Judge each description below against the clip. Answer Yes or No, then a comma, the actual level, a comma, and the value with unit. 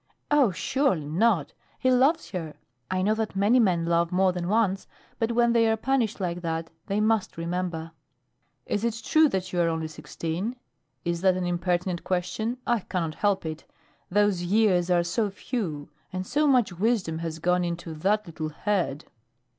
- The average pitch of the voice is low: No, medium, 185 Hz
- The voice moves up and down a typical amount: Yes, average, 4.6 semitones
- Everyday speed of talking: Yes, average, 175 wpm